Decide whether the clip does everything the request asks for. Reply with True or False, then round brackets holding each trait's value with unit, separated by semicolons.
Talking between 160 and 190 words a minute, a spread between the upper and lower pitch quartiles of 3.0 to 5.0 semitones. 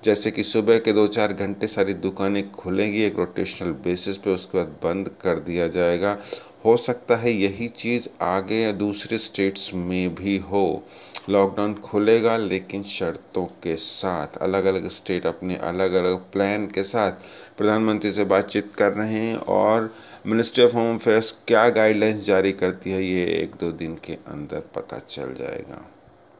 False (165 wpm; 2.5 semitones)